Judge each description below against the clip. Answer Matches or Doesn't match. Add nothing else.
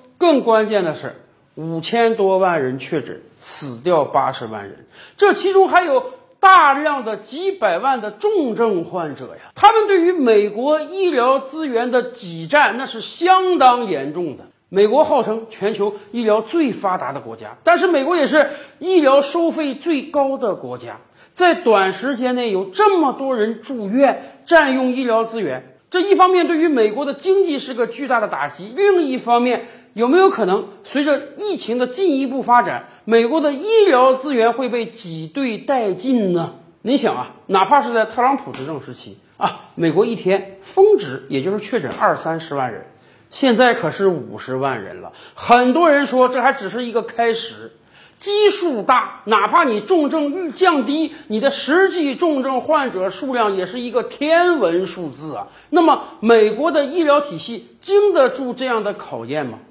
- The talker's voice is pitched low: Doesn't match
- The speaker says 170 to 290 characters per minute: Matches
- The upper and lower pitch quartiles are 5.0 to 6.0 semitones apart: Doesn't match